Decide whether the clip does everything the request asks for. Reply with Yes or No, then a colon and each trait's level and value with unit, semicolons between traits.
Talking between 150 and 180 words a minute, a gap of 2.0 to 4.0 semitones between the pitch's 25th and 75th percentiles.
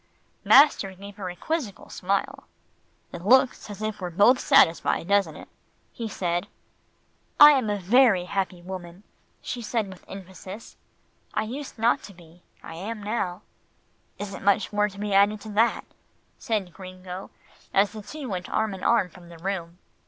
Yes: average, 165 wpm; average, 3.1 semitones